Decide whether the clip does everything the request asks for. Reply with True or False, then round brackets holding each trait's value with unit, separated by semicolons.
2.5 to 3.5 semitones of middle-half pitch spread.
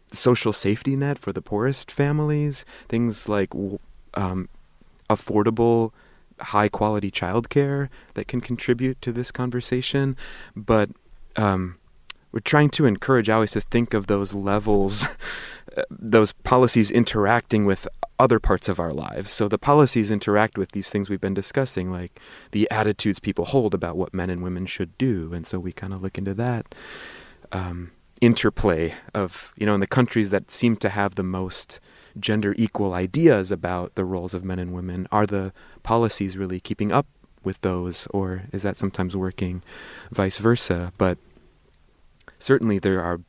False (3.9 semitones)